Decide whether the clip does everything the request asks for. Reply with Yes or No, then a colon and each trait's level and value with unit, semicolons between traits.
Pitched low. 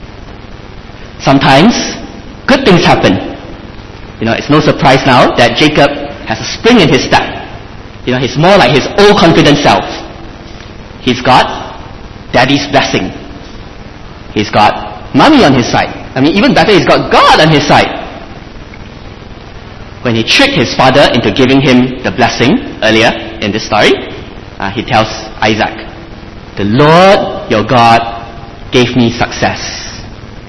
Yes: low, 115 Hz